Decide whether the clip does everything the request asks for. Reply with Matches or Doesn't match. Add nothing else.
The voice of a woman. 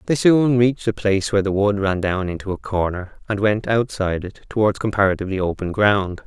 Doesn't match